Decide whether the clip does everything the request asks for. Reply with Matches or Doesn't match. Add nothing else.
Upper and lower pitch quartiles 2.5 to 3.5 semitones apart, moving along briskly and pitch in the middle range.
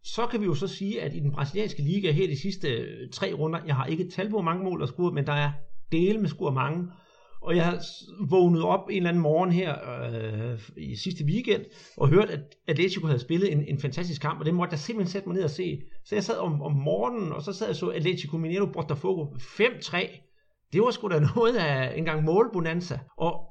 Doesn't match